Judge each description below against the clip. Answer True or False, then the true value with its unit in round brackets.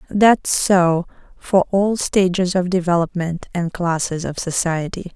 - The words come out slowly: True (130 wpm)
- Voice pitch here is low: False (180 Hz)